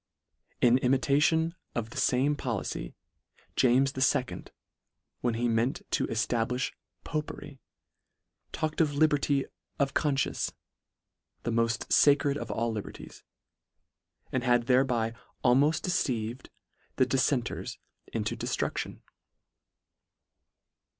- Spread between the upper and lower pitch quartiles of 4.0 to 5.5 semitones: No, average, 3.3 semitones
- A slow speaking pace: Yes, slow, 105 wpm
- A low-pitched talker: Yes, low, 130 Hz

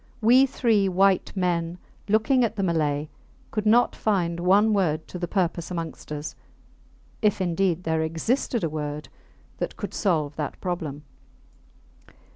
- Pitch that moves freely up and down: No, average, 4.6 semitones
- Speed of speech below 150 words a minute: Yes, average, 140 wpm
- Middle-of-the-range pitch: Yes, medium, 180 Hz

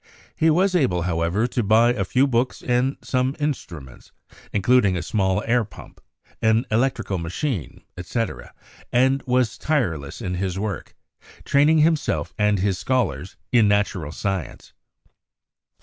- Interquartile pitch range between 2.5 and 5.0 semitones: No, wide, 5.6 semitones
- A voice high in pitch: No, low, 110 Hz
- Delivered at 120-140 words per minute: Yes, slow, 135 wpm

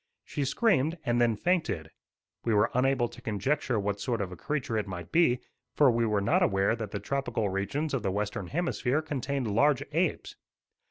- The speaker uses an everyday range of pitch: No, wide, 5.7 semitones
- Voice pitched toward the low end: Yes, low, 120 Hz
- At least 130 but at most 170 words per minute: No, average, 185 wpm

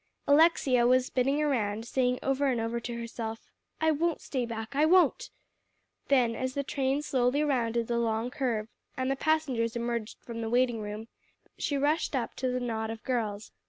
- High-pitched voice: Yes, very high, 250 Hz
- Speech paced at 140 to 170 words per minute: No, average, 180 wpm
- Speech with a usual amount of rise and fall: Yes, average, 3.3 semitones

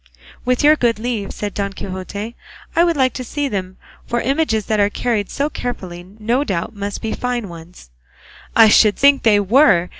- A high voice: Yes, high, 220 Hz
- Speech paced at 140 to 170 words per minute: No, average, 185 wpm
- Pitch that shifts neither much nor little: Yes, average, 4.0 semitones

